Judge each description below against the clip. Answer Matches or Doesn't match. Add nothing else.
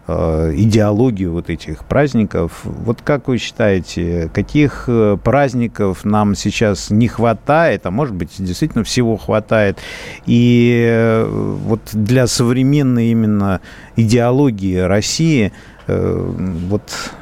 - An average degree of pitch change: Matches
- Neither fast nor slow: Doesn't match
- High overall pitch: Doesn't match